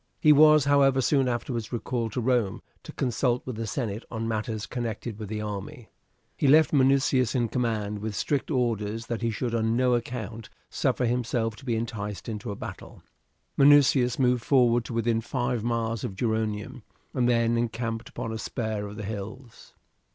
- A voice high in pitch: No, low, 115 Hz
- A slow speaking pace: No, average, 175 wpm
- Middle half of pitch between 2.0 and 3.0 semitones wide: Yes, narrow, 2.4 semitones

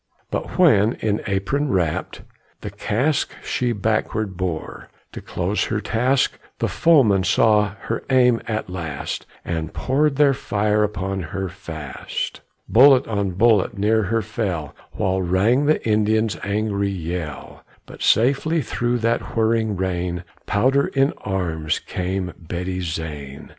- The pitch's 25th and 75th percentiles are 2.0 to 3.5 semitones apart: No, average, 4.3 semitones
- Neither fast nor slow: No, slow, 130 wpm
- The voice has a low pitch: Yes, low, 105 Hz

